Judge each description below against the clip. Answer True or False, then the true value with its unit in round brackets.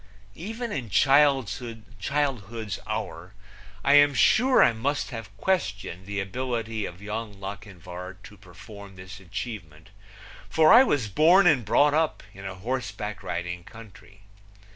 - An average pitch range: False (5.9 semitones)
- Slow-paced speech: True (130 wpm)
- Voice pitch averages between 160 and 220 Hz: False (110 Hz)